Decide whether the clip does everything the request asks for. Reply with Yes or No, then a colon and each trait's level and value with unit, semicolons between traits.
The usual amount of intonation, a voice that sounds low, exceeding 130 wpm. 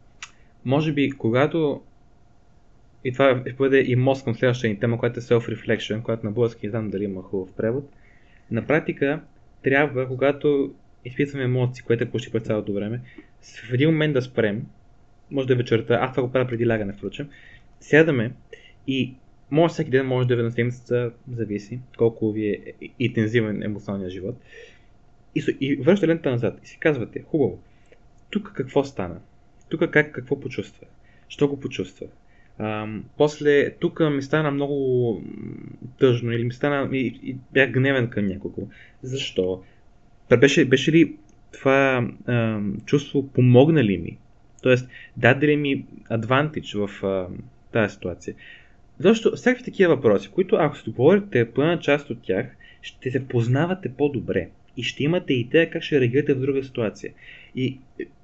Yes: average, 3.8 semitones; low, 125 Hz; average, 160 wpm